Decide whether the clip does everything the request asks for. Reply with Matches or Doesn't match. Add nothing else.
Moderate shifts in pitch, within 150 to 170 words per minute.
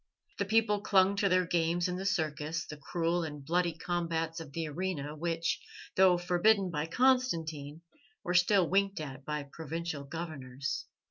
Matches